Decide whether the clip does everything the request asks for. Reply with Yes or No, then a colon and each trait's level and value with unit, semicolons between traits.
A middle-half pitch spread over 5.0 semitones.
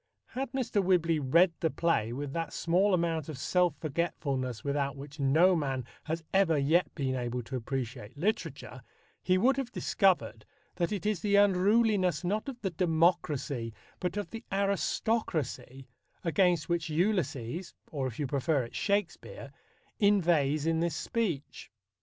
Yes: wide, 5.5 semitones